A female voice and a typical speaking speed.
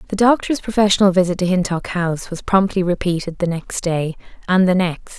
Yes: female; average, 185 wpm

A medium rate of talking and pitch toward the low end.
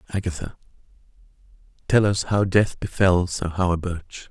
No: slow, 110 wpm; very low, 95 Hz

